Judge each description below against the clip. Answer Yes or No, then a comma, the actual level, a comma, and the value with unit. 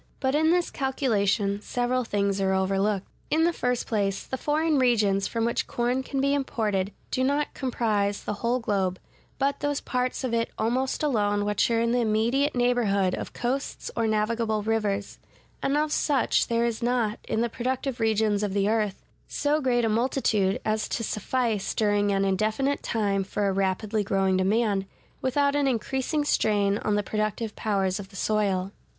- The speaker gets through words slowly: No, average, 175 wpm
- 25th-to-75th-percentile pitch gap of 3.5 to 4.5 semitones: Yes, average, 3.9 semitones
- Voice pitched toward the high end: Yes, high, 220 Hz